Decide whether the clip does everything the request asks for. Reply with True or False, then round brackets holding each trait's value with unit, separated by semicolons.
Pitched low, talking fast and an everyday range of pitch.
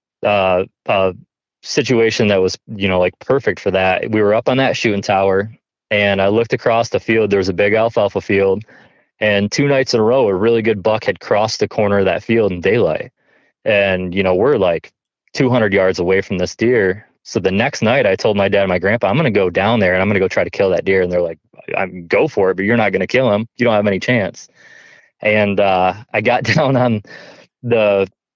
True (105 Hz; 235 wpm; 3.0 semitones)